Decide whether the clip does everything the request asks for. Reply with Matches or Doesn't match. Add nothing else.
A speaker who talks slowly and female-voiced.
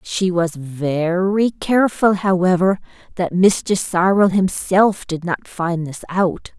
Matches